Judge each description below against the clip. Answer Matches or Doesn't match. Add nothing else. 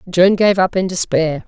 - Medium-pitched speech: Matches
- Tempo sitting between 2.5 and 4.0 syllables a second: Doesn't match